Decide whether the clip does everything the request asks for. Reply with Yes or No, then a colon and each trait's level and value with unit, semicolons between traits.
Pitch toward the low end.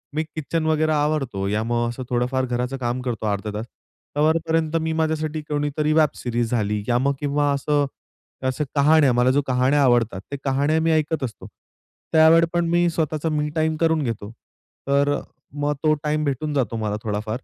No: medium, 145 Hz